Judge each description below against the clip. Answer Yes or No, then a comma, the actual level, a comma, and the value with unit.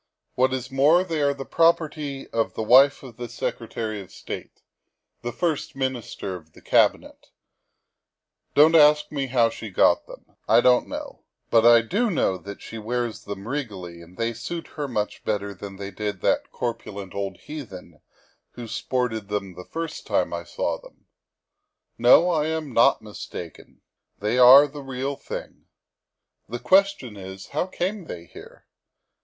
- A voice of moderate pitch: No, low, 125 Hz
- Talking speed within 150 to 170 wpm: Yes, average, 160 wpm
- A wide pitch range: Yes, wide, 6.1 semitones